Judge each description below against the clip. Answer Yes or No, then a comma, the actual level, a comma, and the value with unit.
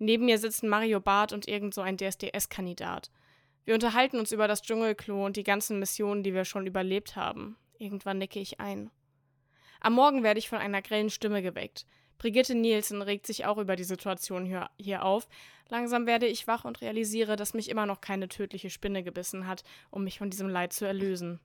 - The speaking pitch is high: Yes, high, 200 Hz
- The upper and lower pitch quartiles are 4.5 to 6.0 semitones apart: No, narrow, 2.6 semitones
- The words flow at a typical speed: No, fast, 195 wpm